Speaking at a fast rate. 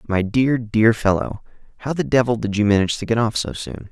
Yes: fast, 230 wpm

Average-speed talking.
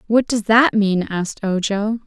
Yes: average, 175 wpm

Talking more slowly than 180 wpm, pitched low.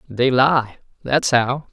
Yes: average, 140 wpm; low, 130 Hz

